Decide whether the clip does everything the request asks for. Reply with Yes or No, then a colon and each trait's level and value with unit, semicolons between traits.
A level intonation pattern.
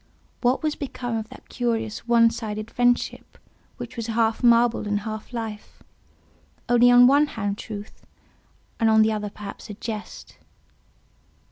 Yes: narrow, 2.1 semitones